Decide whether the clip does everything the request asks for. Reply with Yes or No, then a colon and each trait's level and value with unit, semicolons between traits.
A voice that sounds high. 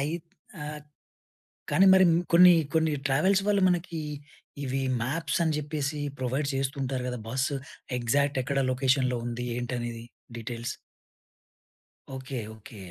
No: low, 135 Hz